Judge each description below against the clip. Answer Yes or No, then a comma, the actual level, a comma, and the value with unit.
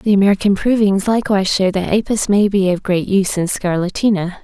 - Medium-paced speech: Yes, average, 190 wpm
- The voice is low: No, high, 195 Hz